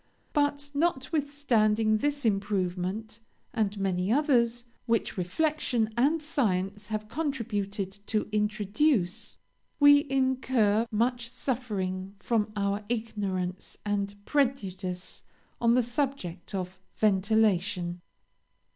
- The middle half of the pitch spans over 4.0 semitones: Yes, average, 4.9 semitones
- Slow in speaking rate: Yes, slow, 95 wpm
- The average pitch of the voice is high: Yes, high, 215 Hz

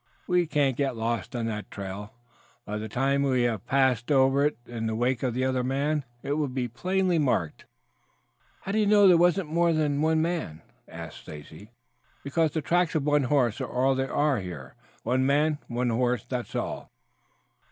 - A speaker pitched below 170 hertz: Yes, low, 135 Hz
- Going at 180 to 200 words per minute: Yes, average, 190 wpm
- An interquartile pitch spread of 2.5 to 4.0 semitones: No, average, 4.4 semitones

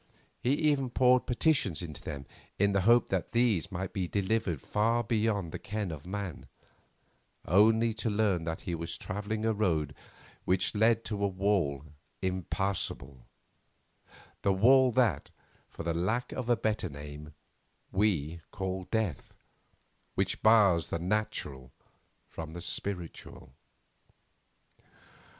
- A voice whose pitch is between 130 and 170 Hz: No, low, 100 Hz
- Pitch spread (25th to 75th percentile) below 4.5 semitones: No, average, 4.9 semitones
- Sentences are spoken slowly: Yes, slow, 130 wpm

